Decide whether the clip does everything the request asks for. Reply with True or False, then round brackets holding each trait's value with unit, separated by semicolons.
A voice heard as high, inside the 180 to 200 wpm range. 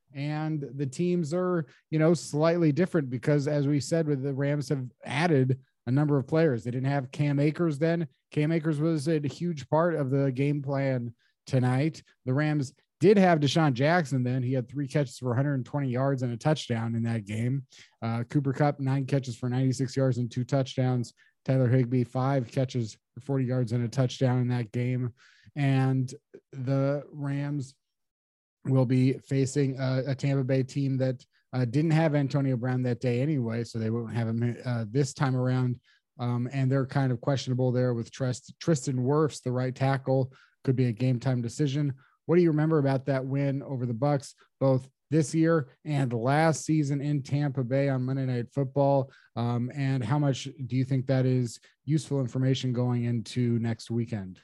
False (135 Hz; 185 wpm)